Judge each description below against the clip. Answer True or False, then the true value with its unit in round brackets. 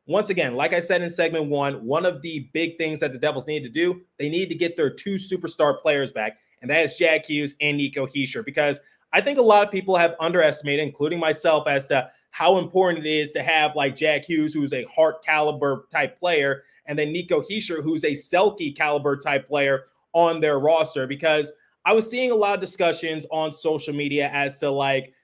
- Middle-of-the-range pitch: True (155 Hz)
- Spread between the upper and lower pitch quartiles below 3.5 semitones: True (3.1 semitones)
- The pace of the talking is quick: True (215 wpm)